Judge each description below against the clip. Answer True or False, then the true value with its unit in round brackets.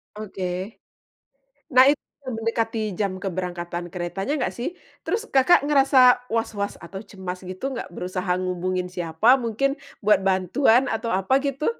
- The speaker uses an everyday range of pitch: False (5.8 semitones)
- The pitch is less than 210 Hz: False (215 Hz)